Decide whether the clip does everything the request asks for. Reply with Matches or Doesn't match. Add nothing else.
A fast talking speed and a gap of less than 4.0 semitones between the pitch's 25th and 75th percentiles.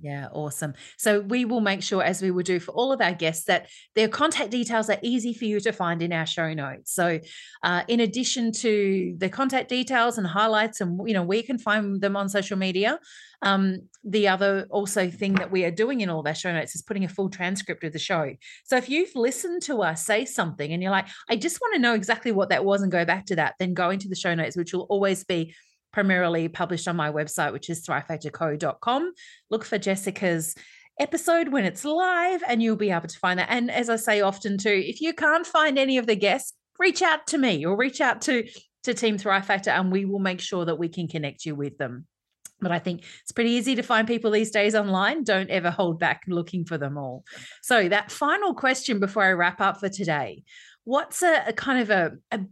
Doesn't match